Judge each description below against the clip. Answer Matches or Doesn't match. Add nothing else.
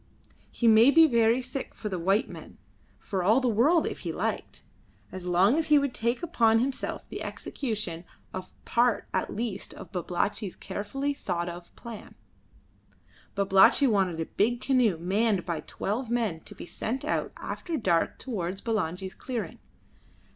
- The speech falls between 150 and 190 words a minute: Matches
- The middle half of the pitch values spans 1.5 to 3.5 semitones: Doesn't match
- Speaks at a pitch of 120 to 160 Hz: Doesn't match